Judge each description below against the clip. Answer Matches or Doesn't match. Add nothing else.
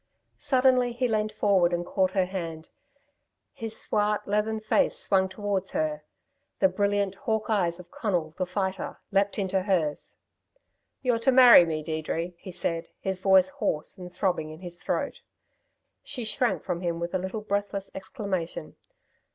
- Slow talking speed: Doesn't match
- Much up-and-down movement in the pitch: Doesn't match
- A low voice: Doesn't match